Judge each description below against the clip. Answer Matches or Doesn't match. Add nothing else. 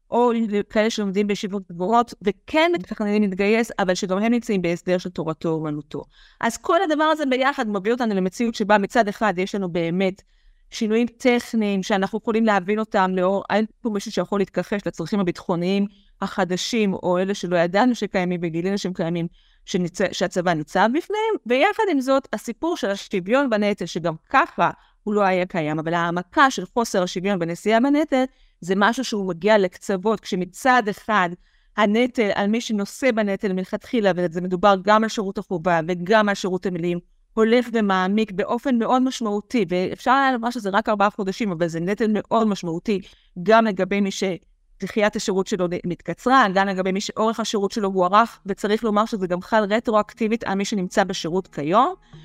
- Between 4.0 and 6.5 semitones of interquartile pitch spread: Doesn't match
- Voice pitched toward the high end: Matches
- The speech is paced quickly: Matches